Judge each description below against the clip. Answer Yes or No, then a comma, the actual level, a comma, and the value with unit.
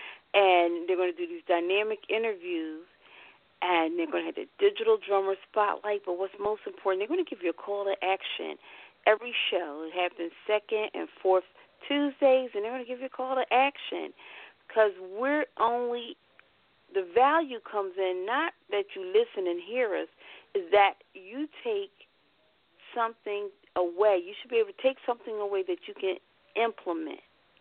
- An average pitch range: No, wide, 7.4 semitones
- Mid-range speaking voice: No, high, 215 Hz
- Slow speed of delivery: No, average, 175 wpm